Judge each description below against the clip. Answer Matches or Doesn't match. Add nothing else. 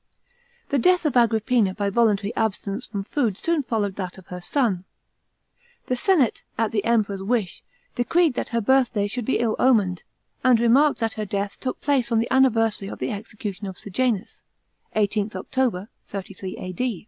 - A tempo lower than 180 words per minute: Matches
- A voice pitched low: Doesn't match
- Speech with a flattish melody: Doesn't match